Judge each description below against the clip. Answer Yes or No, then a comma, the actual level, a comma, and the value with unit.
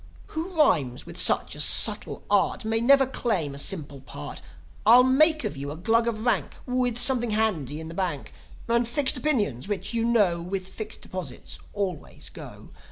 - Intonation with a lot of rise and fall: Yes, wide, 6.6 semitones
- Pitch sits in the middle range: No, high, 215 Hz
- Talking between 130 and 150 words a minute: No, average, 175 wpm